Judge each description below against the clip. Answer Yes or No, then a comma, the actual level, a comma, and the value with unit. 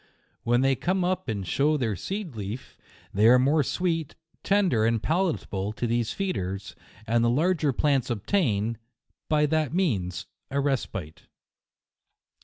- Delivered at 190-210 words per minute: No, average, 140 wpm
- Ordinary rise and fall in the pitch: No, wide, 6.8 semitones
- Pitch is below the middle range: Yes, low, 130 Hz